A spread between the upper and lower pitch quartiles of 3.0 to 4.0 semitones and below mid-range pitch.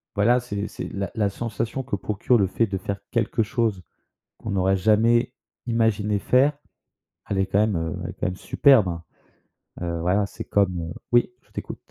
Yes: average, 3.3 semitones; low, 105 Hz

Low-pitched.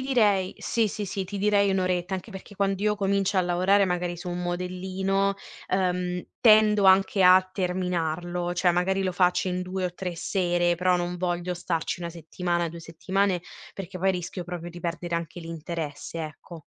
No: medium, 180 Hz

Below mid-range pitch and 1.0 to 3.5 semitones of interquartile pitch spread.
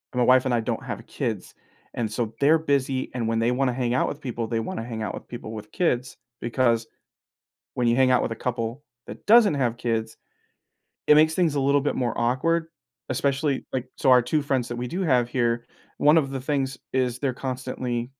Yes: low, 125 Hz; average, 2.7 semitones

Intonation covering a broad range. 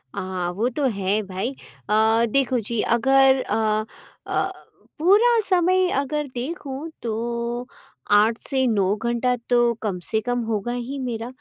No: average, 3.9 semitones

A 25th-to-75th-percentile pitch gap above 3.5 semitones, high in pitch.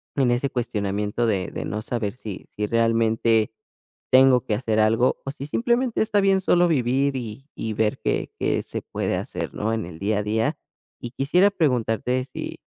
No: average, 4.0 semitones; low, 120 Hz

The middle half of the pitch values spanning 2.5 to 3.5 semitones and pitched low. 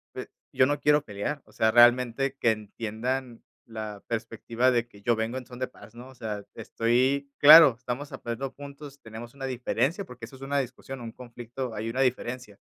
Yes: average, 2.8 semitones; low, 125 Hz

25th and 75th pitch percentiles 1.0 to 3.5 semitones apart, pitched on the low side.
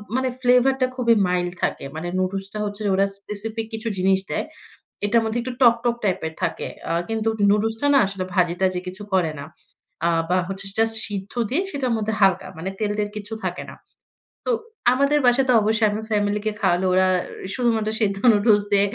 No: average, 3.2 semitones; high, 210 Hz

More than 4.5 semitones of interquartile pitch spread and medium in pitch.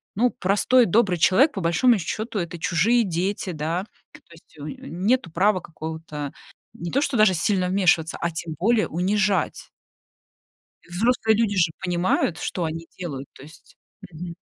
No: average, 4.1 semitones; medium, 180 Hz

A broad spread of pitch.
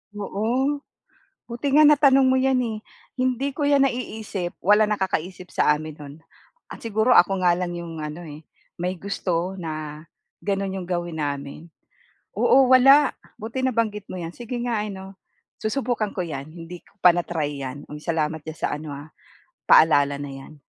Yes: wide, 6.9 semitones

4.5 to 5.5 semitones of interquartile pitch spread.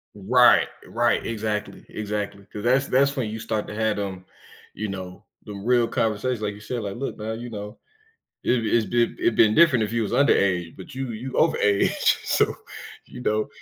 No: average, 2.9 semitones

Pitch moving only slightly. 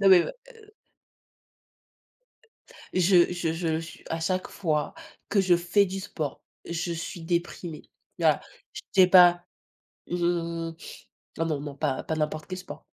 Yes: narrow, 2.1 semitones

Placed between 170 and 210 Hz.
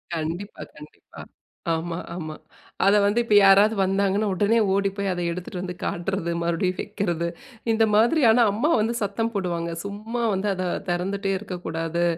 Yes: high, 195 Hz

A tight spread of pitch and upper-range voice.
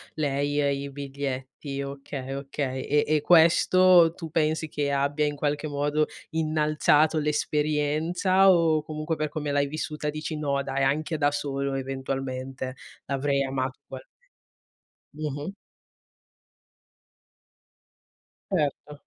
No: narrow, 2.0 semitones; medium, 145 Hz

